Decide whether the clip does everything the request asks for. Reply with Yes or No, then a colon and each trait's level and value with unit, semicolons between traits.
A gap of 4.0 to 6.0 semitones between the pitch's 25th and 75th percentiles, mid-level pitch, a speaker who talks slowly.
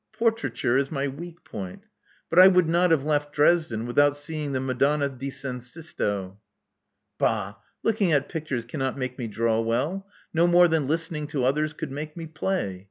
No: average, 4.3 semitones; medium, 145 Hz; average, 175 wpm